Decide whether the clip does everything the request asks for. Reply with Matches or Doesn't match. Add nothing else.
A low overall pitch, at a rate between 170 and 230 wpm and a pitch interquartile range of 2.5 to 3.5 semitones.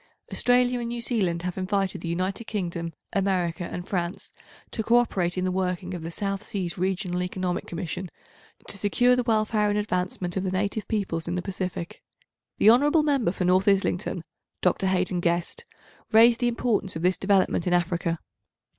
Doesn't match